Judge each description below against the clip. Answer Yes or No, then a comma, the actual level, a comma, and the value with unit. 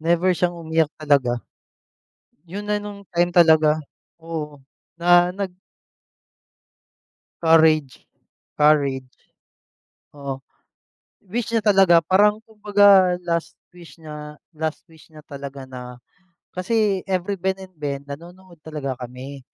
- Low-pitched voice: No, medium, 165 Hz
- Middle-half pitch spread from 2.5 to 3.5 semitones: No, average, 4.0 semitones